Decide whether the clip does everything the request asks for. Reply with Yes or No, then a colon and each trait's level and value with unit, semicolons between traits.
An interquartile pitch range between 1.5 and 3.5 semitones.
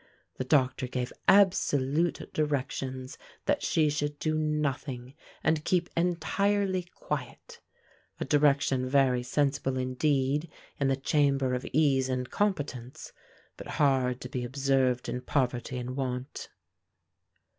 Yes: average, 3.0 semitones